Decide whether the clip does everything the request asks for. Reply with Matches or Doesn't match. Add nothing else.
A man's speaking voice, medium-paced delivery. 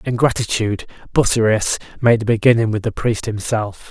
Matches